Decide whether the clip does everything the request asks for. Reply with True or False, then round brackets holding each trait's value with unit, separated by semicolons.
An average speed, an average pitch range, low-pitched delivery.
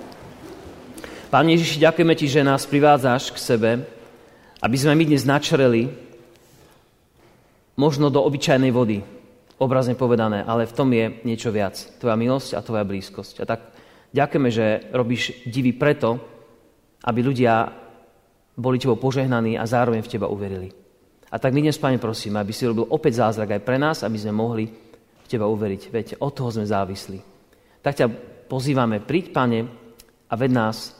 True (155 wpm; 3.1 semitones; 120 Hz)